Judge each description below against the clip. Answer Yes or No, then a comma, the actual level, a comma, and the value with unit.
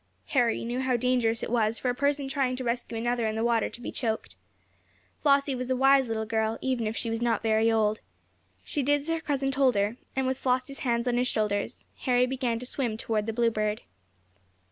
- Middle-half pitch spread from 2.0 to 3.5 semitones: Yes, average, 2.7 semitones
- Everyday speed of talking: No, fast, 215 wpm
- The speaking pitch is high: Yes, high, 240 Hz